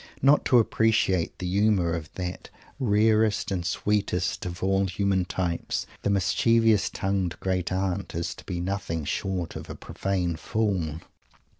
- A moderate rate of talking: Yes, average, 145 wpm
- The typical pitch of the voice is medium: No, very low, 95 Hz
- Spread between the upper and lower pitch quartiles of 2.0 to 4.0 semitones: Yes, average, 2.8 semitones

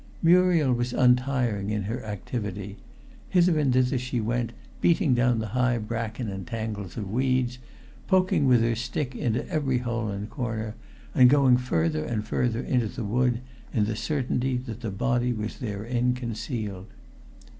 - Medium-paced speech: Yes, average, 155 wpm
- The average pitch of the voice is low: Yes, low, 120 Hz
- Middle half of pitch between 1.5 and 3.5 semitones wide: Yes, average, 2.8 semitones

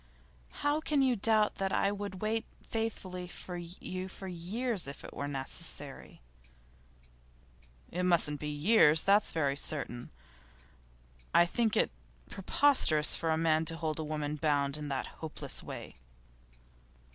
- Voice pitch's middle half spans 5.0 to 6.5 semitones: Yes, average, 5.3 semitones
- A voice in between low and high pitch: Yes, medium, 175 Hz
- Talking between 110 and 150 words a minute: Yes, average, 140 wpm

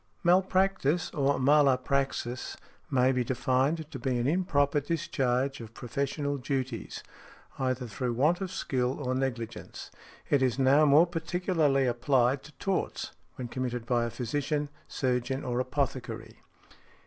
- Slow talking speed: Yes, slow, 130 wpm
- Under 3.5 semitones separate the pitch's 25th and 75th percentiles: Yes, average, 2.9 semitones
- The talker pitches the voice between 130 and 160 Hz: Yes, low, 135 Hz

